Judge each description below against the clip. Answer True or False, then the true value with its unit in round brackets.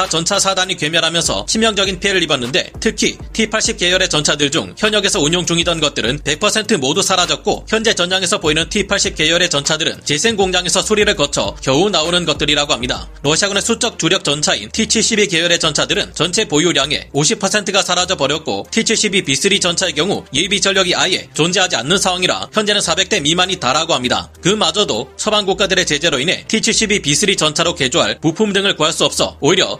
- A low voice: False (185 Hz)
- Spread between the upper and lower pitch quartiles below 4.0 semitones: False (4.5 semitones)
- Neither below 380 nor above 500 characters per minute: True (395 characters per minute)